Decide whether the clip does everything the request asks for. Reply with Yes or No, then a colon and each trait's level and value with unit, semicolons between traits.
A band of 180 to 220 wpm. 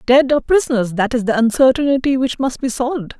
Yes: fast, 205 wpm